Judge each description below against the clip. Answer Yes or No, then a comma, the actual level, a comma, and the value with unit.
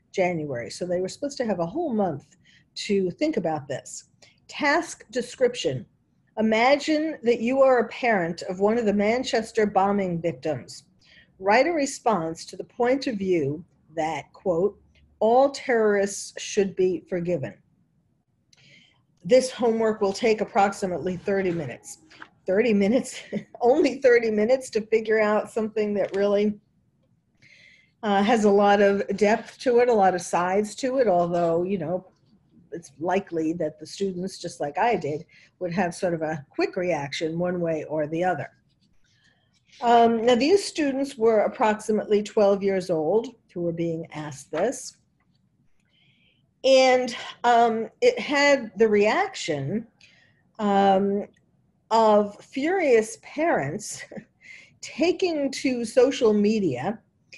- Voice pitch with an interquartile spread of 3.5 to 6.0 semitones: Yes, wide, 5.4 semitones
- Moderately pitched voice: No, high, 205 Hz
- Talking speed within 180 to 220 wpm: No, slow, 135 wpm